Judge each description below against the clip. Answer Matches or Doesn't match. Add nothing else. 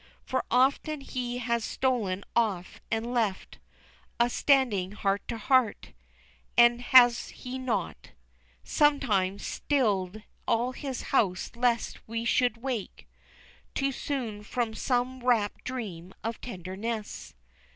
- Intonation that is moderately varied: Matches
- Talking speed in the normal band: Doesn't match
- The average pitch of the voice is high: Matches